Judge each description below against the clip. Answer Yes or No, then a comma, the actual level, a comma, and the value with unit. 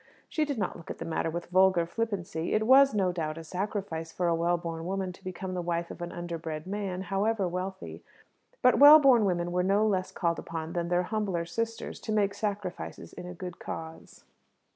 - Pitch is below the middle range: No, medium, 180 Hz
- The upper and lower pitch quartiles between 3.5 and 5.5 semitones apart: No, average, 3.1 semitones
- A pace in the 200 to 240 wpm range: Yes, fast, 205 wpm